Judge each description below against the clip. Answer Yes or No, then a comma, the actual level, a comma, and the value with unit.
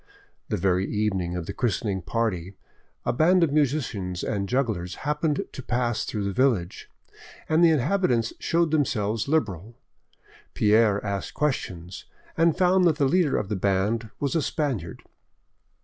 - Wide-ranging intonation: Yes, wide, 7.3 semitones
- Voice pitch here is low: Yes, low, 115 Hz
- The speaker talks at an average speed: Yes, average, 150 wpm